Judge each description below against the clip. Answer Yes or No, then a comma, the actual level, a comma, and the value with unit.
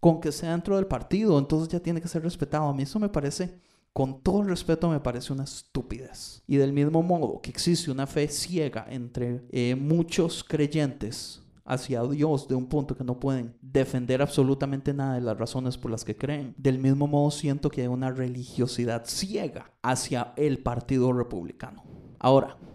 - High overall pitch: No, medium, 140 Hz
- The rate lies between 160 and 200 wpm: Yes, average, 185 wpm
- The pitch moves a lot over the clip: No, average, 3.8 semitones